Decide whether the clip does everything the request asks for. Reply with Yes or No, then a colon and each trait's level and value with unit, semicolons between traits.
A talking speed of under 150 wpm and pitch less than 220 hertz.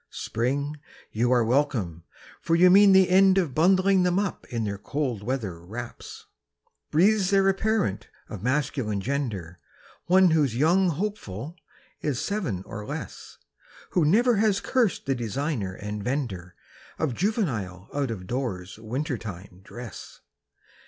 Yes: average, 140 wpm; low, 135 Hz